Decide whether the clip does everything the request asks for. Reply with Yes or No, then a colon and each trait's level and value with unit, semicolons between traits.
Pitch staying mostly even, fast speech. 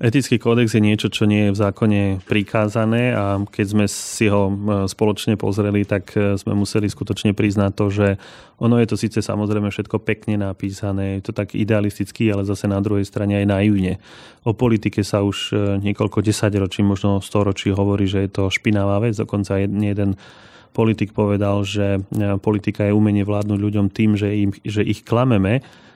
Yes: narrow, 1.3 semitones; fast, 170 wpm